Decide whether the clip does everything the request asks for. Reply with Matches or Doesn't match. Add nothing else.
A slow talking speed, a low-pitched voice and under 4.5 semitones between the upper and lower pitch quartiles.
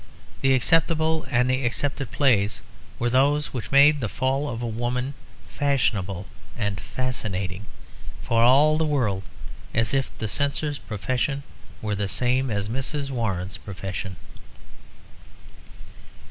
Doesn't match